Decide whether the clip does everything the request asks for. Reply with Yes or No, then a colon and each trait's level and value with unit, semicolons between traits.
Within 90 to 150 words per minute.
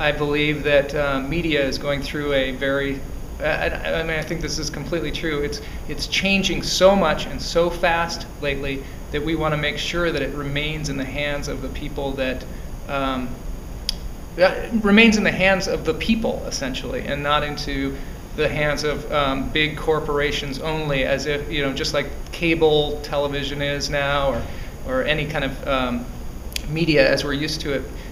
No: average, 185 wpm